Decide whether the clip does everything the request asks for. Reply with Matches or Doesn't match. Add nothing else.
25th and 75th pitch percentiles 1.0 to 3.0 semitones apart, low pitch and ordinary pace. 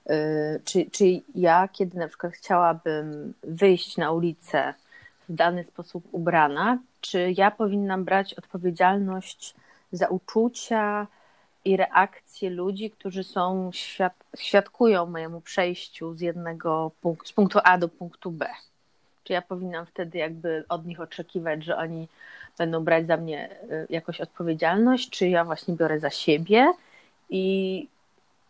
Doesn't match